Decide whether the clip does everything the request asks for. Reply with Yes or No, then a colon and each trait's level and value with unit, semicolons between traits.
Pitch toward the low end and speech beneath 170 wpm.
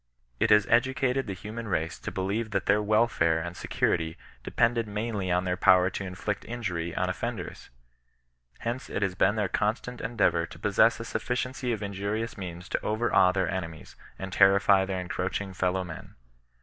No: low, 100 Hz; average, 175 wpm